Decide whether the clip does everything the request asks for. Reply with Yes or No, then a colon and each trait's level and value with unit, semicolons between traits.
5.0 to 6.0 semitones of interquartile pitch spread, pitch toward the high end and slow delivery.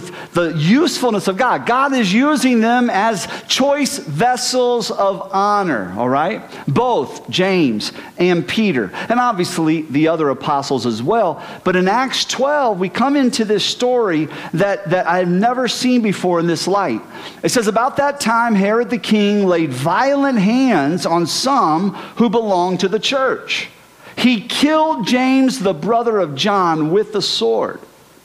No: wide, 5.5 semitones; high, 210 Hz; average, 155 wpm